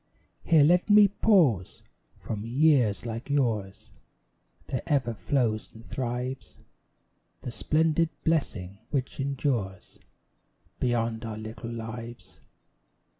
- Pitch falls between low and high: No, low, 120 Hz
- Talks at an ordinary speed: No, slow, 100 wpm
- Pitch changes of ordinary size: Yes, average, 4.5 semitones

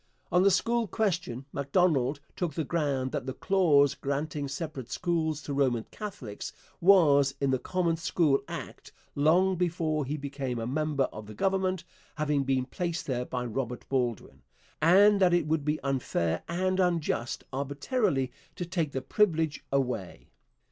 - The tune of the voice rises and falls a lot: No, average, 4.7 semitones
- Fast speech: No, average, 155 wpm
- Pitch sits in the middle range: Yes, medium, 150 Hz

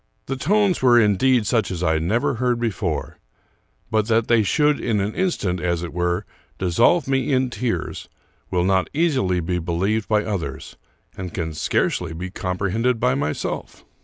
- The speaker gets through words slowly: No, average, 160 wpm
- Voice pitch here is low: Yes, low, 105 Hz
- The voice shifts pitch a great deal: Yes, wide, 6.0 semitones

